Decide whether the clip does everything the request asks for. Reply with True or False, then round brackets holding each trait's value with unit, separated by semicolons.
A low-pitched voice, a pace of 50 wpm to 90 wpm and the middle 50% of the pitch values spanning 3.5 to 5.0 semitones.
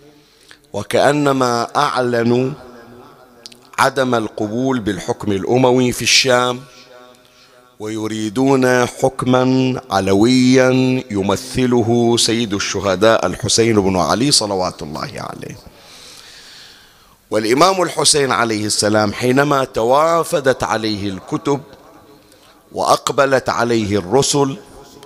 False (125 Hz; 75 wpm; 3.0 semitones)